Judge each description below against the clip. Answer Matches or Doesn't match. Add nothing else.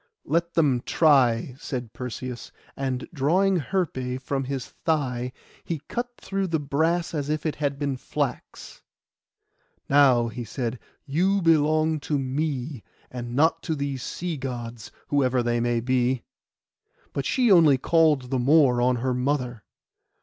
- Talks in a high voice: Doesn't match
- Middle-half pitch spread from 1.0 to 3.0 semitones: Doesn't match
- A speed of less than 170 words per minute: Matches